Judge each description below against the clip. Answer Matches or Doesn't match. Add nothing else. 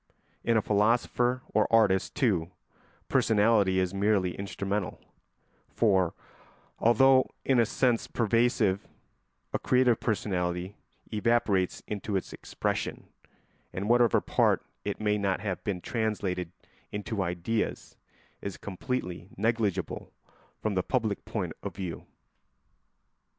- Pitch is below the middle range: Matches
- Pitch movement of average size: Matches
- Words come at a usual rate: Doesn't match